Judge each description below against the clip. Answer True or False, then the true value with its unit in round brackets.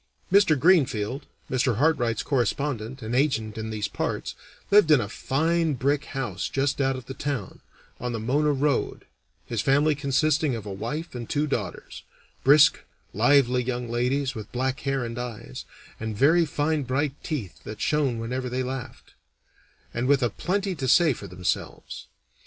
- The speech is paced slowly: False (165 wpm)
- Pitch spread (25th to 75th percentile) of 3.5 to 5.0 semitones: True (3.9 semitones)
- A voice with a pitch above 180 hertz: False (130 Hz)